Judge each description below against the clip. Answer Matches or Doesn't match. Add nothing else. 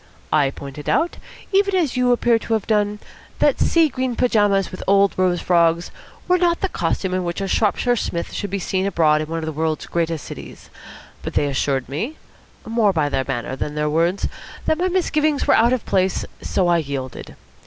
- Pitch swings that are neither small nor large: Doesn't match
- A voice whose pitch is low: Doesn't match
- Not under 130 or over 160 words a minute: Doesn't match